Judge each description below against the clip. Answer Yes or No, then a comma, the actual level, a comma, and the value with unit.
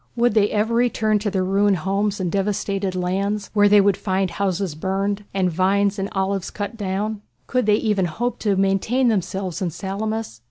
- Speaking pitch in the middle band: No, high, 200 Hz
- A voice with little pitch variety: Yes, narrow, 1.7 semitones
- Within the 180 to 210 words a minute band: Yes, average, 185 wpm